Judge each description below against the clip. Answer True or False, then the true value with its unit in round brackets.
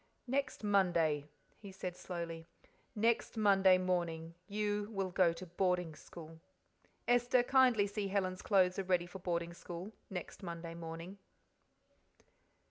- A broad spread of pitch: False (3.2 semitones)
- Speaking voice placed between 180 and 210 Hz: True (185 Hz)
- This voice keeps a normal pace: False (130 wpm)